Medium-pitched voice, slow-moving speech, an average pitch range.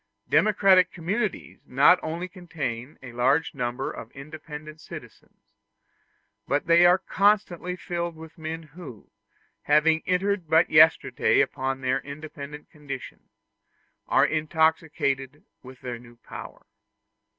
Yes: medium, 155 Hz; slow, 115 wpm; average, 4.0 semitones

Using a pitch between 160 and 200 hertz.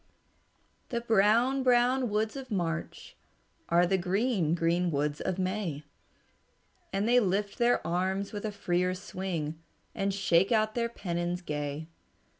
Yes: high, 190 Hz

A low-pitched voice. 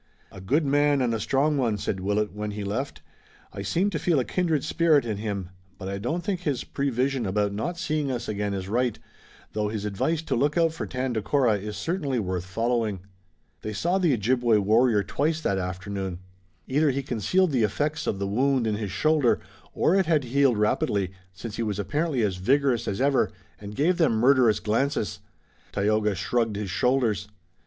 Yes: low, 120 Hz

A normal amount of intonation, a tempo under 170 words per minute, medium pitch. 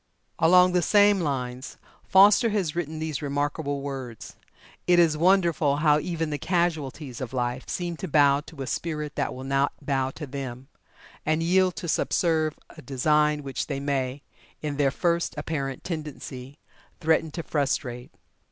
Yes: average, 3.4 semitones; average, 155 wpm; medium, 150 Hz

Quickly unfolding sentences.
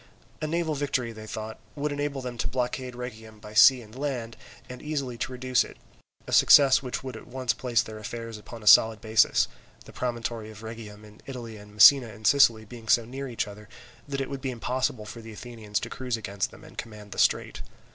Yes: fast, 215 wpm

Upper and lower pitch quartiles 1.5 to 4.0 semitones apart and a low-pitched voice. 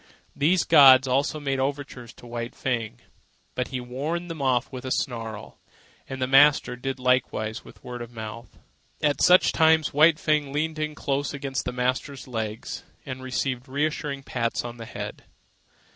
Yes: average, 2.9 semitones; low, 130 Hz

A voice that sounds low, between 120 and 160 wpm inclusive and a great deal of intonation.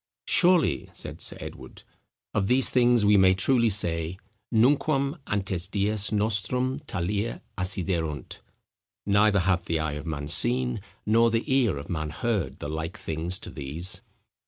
Yes: low, 100 Hz; average, 145 wpm; wide, 5.8 semitones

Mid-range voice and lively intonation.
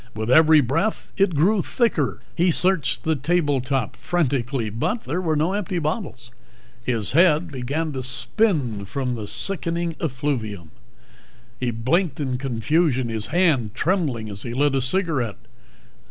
Yes: medium, 145 Hz; wide, 5.9 semitones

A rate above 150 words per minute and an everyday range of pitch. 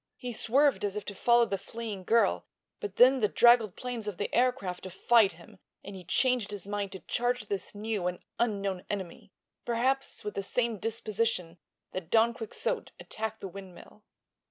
Yes: average, 170 wpm; average, 3.4 semitones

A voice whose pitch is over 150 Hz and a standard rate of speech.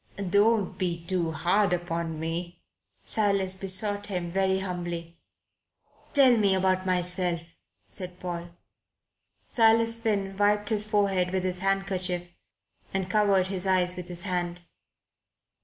No: medium, 185 Hz; slow, 125 wpm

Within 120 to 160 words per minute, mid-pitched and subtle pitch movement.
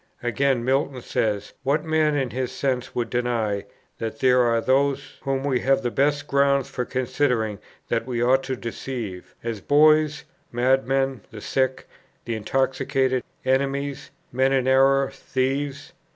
No: average, 145 wpm; low, 130 Hz; narrow, 2.2 semitones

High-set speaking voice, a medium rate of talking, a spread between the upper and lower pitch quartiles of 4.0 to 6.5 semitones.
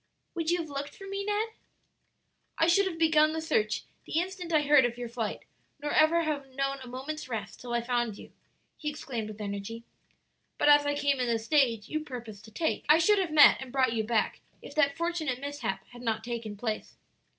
No: very high, 275 Hz; fast, 215 wpm; average, 5.1 semitones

